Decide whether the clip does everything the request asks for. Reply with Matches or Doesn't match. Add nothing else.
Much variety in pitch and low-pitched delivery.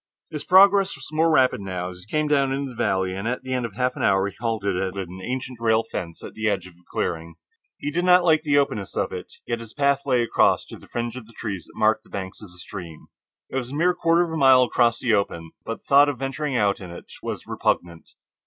Matches